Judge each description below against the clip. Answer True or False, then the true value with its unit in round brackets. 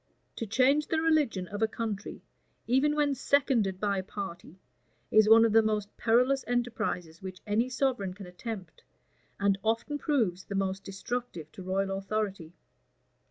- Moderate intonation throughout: True (4.3 semitones)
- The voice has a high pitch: True (215 Hz)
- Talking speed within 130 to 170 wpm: True (155 wpm)